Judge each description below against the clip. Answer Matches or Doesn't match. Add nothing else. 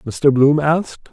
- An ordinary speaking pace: Matches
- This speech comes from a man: Matches